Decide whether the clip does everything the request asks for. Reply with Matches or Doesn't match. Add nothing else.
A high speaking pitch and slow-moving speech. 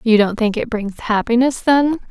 Doesn't match